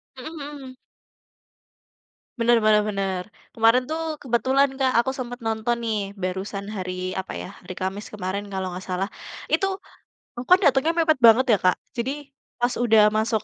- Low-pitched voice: No, high, 225 Hz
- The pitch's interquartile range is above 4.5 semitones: Yes, average, 4.9 semitones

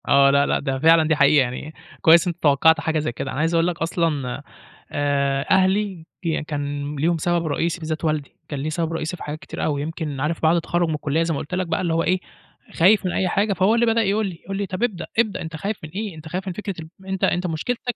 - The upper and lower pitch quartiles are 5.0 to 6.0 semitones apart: No, average, 3.7 semitones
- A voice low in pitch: No, medium, 165 Hz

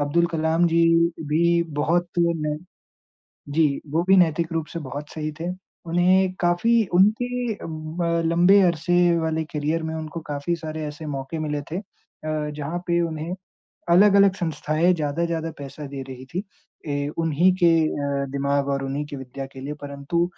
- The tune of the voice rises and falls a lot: No, average, 2.8 semitones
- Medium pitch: Yes, medium, 160 Hz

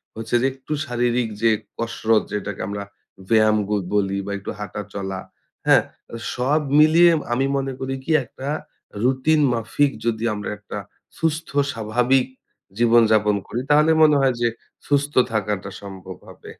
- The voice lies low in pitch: Yes, low, 120 Hz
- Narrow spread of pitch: No, average, 4.3 semitones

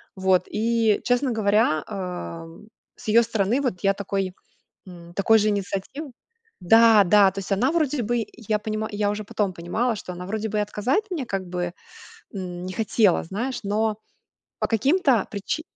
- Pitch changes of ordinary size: Yes, average, 3.2 semitones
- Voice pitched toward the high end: Yes, high, 210 Hz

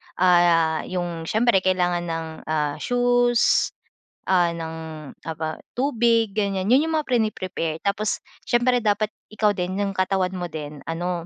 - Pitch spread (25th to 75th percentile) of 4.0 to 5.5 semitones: Yes, average, 4.7 semitones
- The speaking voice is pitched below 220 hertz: Yes, medium, 185 Hz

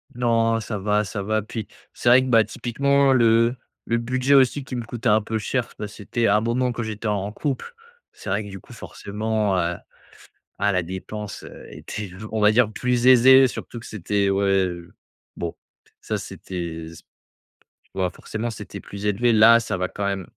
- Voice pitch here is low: Yes, low, 110 Hz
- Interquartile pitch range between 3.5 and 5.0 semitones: No, average, 3.0 semitones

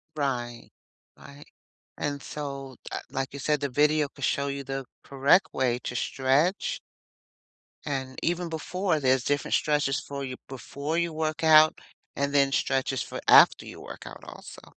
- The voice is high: No, medium, 140 Hz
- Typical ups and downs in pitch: No, narrow, 2.3 semitones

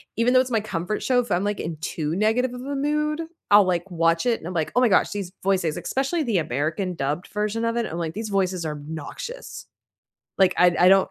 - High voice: Yes, high, 195 Hz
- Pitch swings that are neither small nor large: No, wide, 6.1 semitones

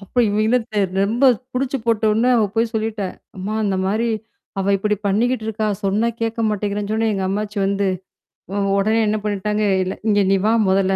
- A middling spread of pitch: No, narrow, 2.2 semitones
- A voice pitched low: No, high, 210 Hz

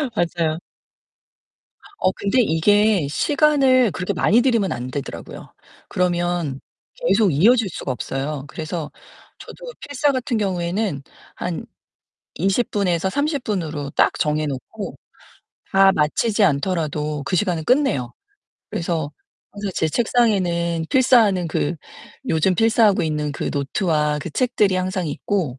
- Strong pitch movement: Yes, wide, 5.9 semitones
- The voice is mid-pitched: Yes, medium, 180 Hz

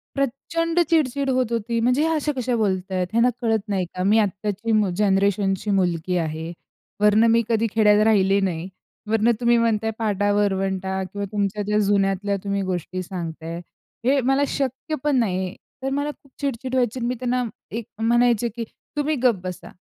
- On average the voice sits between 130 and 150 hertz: No, high, 215 Hz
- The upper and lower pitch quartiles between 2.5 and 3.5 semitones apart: No, average, 4.2 semitones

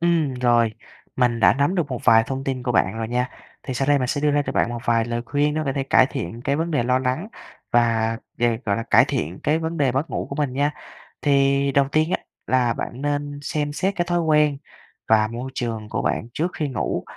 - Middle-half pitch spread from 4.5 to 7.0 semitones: No, average, 3.7 semitones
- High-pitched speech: No, low, 135 Hz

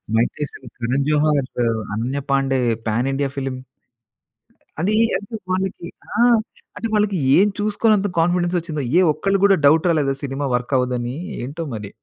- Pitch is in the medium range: Yes, medium, 145 Hz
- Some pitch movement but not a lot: No, wide, 6.0 semitones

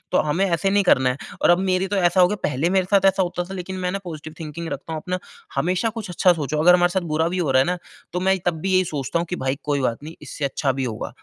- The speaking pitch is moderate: Yes, medium, 175 Hz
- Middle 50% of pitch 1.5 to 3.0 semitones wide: No, average, 3.5 semitones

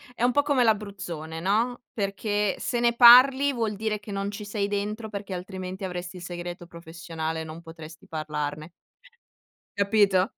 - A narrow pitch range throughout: No, average, 4.2 semitones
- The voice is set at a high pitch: Yes, high, 200 Hz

